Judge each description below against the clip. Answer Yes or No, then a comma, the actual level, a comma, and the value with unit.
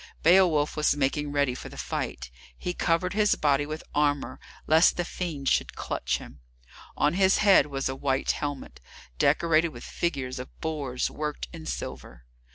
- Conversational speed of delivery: Yes, average, 165 wpm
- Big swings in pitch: No, average, 3.5 semitones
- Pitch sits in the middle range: Yes, medium, 150 Hz